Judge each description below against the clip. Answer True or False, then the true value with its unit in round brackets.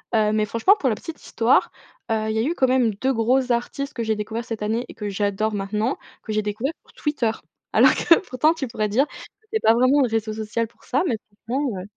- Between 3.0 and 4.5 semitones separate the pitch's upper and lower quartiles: True (3.4 semitones)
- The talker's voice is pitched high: True (230 Hz)